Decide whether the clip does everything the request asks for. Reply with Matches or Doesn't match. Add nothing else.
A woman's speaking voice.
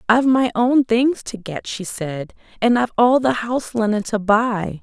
Matches